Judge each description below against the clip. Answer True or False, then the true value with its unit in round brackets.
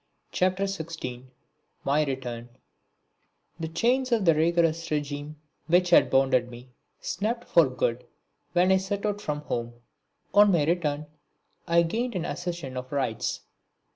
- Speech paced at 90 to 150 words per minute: True (140 wpm)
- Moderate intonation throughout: True (4.9 semitones)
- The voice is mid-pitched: True (165 Hz)